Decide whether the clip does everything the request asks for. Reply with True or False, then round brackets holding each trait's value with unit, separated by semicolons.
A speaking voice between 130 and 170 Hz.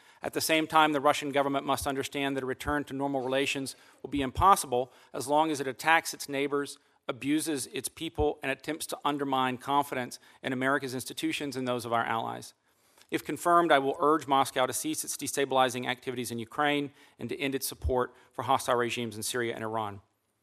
True (140 Hz)